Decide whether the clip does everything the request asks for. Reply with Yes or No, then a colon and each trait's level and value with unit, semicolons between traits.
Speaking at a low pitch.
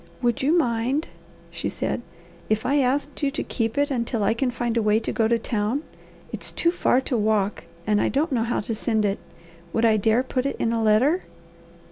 No: high, 235 Hz